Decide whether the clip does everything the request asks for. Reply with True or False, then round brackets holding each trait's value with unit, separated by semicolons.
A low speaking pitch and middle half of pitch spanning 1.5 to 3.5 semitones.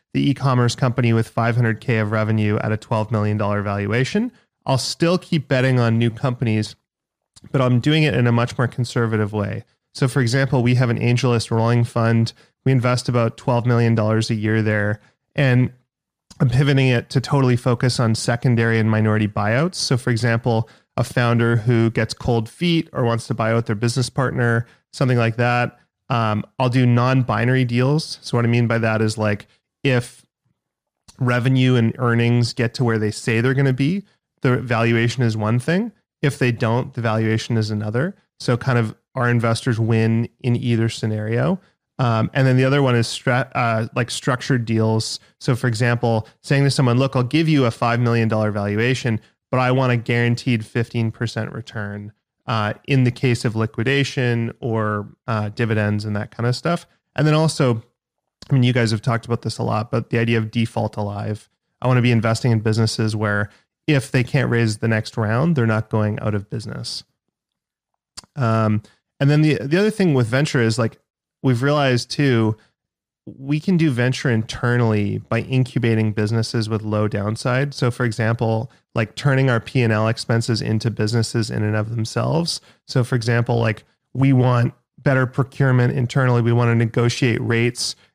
True (120 Hz; 2.5 semitones)